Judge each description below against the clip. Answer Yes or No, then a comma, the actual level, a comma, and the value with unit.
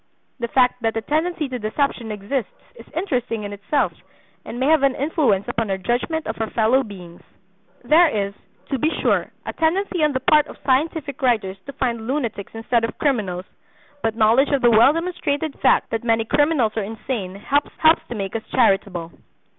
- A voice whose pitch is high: Yes, high, 240 Hz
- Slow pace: No, average, 185 wpm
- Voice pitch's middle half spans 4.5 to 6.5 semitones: Yes, average, 4.9 semitones